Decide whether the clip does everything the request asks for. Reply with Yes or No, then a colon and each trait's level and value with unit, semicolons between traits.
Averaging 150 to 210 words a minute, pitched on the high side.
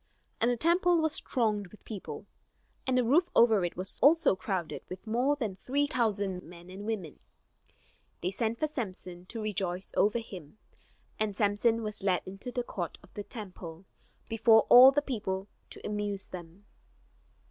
Yes: average, 165 wpm; high, 210 Hz